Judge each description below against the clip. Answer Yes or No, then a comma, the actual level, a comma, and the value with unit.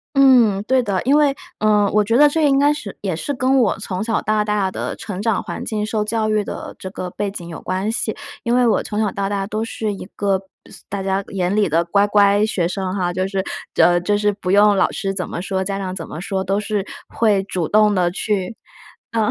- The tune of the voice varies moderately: No, narrow, 2.3 semitones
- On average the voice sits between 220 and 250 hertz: No, high, 205 Hz